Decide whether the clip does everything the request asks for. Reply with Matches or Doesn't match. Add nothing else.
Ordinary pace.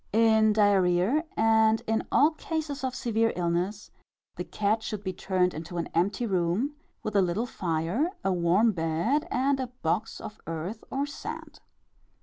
Matches